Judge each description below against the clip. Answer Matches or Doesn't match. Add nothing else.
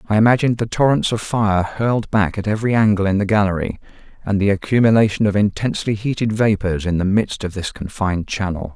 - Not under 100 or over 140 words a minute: Doesn't match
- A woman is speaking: Doesn't match